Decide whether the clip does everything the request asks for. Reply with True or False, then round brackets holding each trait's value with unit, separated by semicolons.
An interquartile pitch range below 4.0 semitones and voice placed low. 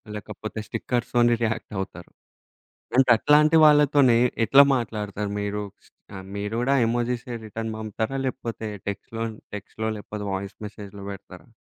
True (3.1 semitones; 110 Hz)